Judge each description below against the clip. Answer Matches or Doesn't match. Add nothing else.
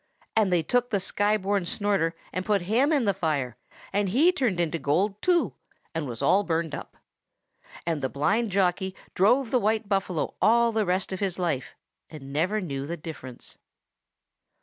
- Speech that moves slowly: Doesn't match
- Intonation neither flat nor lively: Matches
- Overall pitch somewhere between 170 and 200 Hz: Matches